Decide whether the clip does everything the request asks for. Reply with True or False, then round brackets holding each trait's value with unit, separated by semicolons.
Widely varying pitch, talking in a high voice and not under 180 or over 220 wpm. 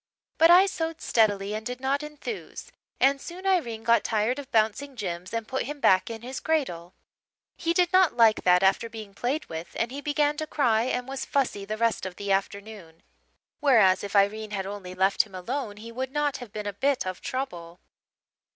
True (5.8 semitones; 230 Hz; 200 wpm)